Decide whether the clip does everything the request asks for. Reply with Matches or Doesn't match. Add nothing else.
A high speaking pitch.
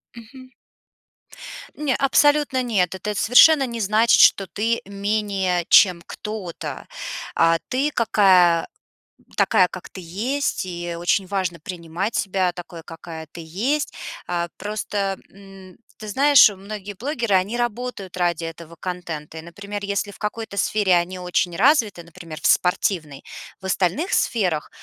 Matches